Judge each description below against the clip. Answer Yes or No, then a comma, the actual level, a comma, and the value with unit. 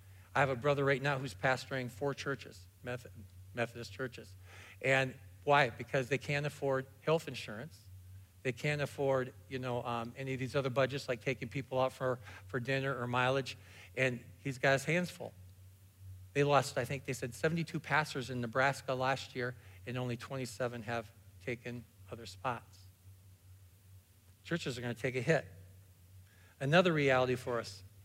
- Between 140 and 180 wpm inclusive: Yes, average, 165 wpm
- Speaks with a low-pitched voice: Yes, low, 125 Hz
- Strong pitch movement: Yes, wide, 5.8 semitones